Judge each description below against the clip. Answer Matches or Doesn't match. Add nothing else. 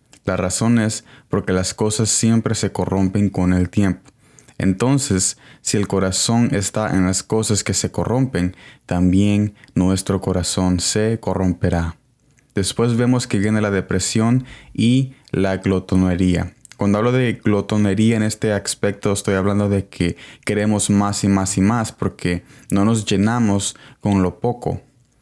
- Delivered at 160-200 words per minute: Doesn't match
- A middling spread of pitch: Matches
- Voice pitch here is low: Matches